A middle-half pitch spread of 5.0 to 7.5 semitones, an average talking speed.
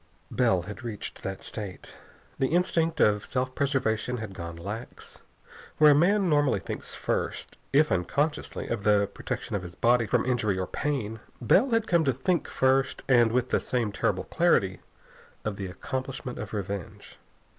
Yes: wide, 5.5 semitones; average, 165 wpm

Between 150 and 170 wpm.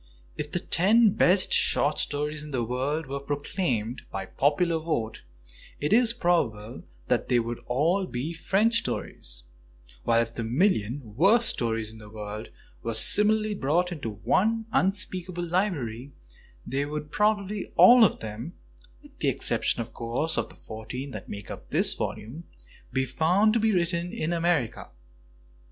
Yes: average, 160 wpm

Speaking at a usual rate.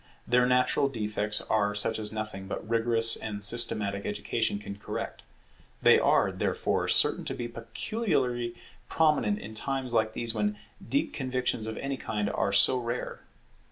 Yes: average, 155 wpm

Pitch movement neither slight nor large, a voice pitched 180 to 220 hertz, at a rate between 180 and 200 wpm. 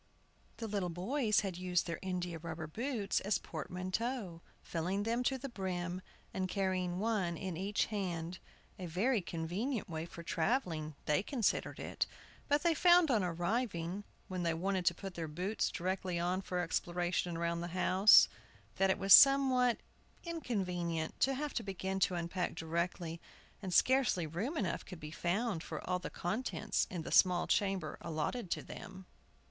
No: average, 3.8 semitones; medium, 185 Hz; average, 165 wpm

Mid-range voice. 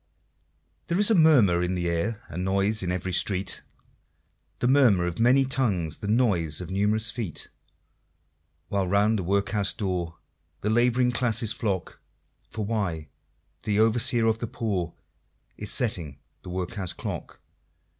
No: low, 100 Hz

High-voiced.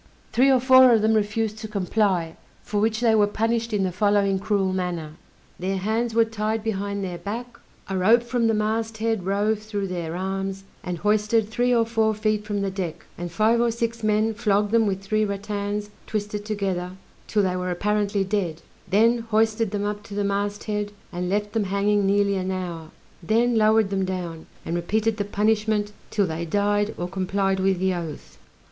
Yes: high, 205 Hz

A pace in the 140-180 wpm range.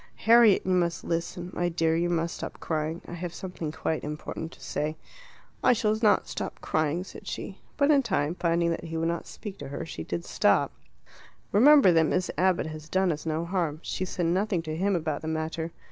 No: fast, 205 wpm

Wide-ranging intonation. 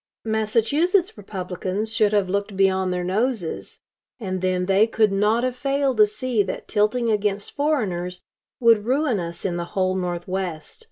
No: average, 3.6 semitones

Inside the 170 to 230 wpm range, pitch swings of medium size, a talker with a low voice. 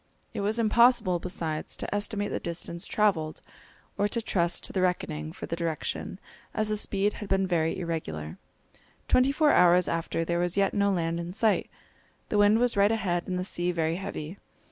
No: average, 190 wpm; average, 3.5 semitones; medium, 185 Hz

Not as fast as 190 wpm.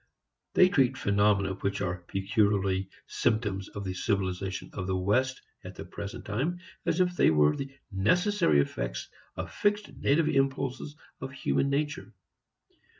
Yes: average, 145 wpm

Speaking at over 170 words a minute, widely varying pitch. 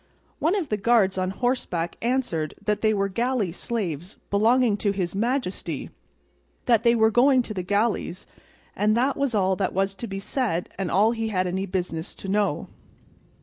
No: average, 180 wpm; average, 3.9 semitones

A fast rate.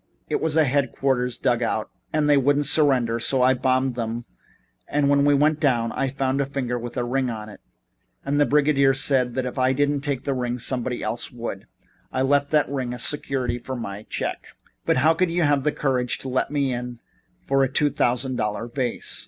Yes: fast, 210 wpm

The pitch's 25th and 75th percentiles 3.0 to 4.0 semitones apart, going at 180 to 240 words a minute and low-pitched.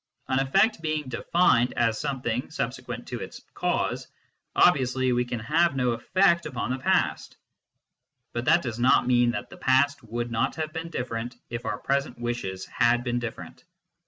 No: average, 3.7 semitones; average, 170 wpm; low, 125 Hz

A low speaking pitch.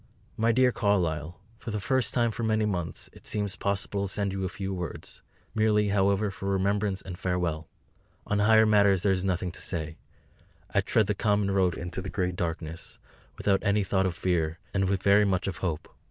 Yes: very low, 95 Hz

